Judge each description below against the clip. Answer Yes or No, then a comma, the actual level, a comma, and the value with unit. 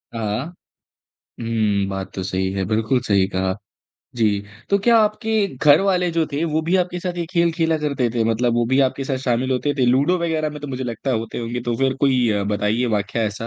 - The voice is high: No, low, 125 Hz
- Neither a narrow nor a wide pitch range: No, wide, 6.3 semitones